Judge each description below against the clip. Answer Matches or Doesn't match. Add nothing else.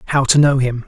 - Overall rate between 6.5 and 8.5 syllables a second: Matches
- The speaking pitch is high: Doesn't match